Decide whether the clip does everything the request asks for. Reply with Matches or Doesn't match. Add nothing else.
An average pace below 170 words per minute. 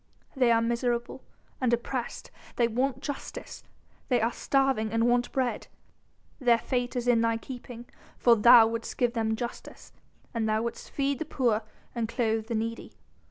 Matches